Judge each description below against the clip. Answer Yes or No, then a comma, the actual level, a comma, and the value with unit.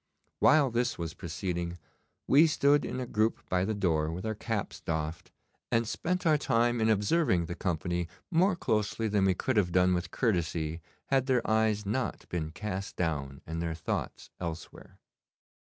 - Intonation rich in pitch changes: Yes, wide, 5.7 semitones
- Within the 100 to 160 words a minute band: No, average, 170 wpm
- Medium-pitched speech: No, low, 100 Hz